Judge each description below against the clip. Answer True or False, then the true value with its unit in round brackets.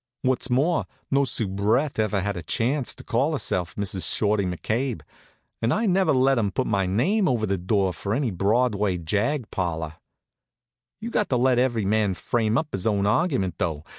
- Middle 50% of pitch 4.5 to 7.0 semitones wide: True (5.2 semitones)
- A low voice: True (110 Hz)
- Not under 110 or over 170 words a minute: False (180 wpm)